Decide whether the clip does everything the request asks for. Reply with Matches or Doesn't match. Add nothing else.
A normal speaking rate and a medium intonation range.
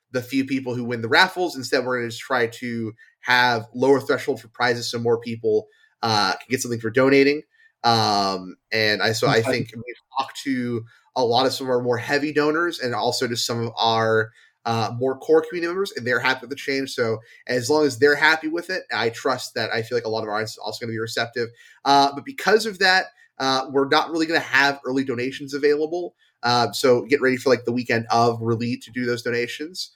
Doesn't match